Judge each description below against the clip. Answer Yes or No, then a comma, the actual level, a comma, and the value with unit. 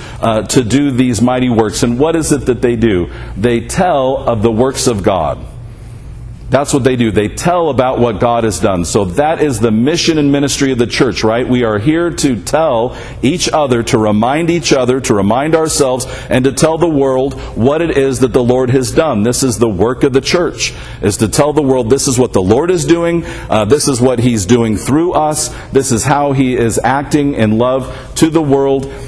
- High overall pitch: No, low, 130 Hz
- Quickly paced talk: Yes, fast, 220 wpm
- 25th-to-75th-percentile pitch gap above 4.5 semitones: No, average, 3.2 semitones